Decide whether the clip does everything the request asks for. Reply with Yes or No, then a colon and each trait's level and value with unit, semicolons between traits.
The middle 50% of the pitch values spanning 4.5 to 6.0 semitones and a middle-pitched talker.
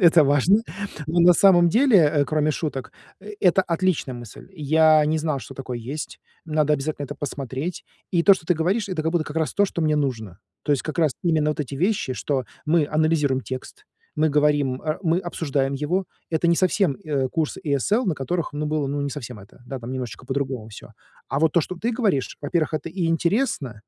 No: average, 3.7 semitones; medium, 155 Hz